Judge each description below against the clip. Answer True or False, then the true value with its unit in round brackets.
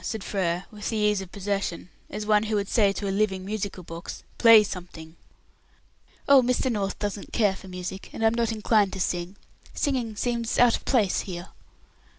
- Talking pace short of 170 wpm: False (185 wpm)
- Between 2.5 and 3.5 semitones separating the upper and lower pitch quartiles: True (2.8 semitones)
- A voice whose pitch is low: False (205 Hz)